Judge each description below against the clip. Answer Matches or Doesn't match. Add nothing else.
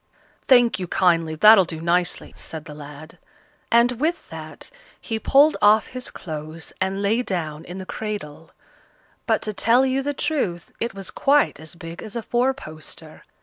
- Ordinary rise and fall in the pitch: Doesn't match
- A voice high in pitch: Matches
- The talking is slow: Doesn't match